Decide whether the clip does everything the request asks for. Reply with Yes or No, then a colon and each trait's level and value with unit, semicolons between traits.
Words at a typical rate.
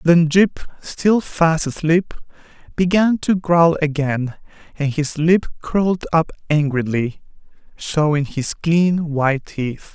No: slow, 120 wpm